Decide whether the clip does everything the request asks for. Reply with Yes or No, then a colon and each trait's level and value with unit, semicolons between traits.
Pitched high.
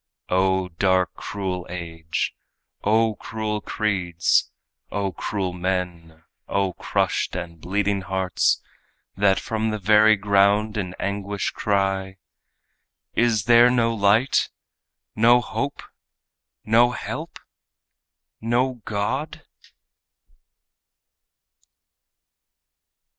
No: low, 100 Hz